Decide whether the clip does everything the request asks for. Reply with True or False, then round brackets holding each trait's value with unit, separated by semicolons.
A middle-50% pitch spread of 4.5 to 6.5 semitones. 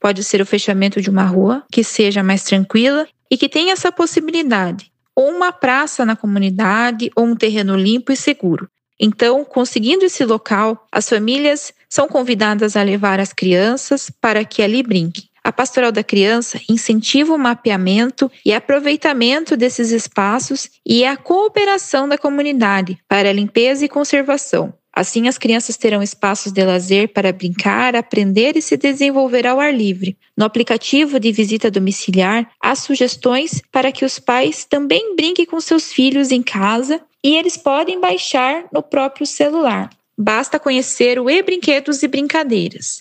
True (5.4 semitones)